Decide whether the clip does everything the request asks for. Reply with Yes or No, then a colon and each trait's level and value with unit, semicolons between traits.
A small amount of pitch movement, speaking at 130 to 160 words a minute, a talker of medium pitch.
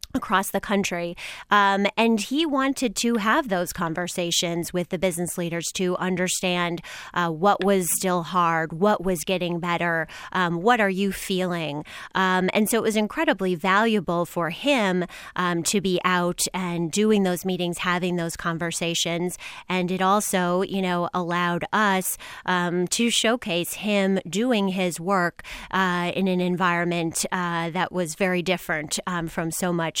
Yes: narrow, 2.2 semitones; average, 155 wpm; medium, 180 Hz